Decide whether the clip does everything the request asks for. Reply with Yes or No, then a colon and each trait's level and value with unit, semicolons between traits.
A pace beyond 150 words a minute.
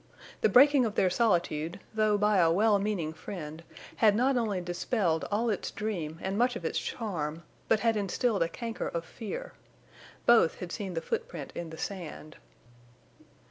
Yes: average, 170 wpm